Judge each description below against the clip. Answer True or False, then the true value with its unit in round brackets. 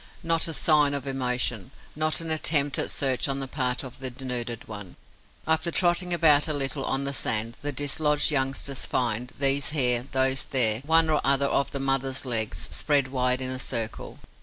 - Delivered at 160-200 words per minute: True (185 wpm)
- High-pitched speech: False (135 Hz)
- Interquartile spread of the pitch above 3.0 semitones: False (2.7 semitones)